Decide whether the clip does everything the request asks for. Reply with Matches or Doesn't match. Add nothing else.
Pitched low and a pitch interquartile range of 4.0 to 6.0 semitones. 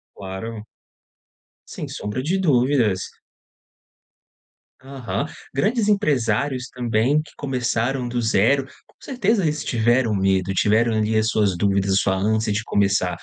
Matches